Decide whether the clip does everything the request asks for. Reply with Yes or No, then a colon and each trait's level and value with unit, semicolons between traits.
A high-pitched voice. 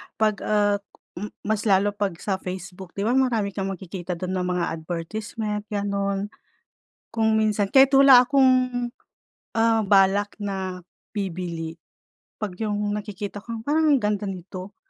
Yes: high, 205 Hz